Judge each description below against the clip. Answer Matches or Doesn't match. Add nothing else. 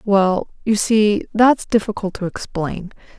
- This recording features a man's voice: Doesn't match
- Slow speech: Matches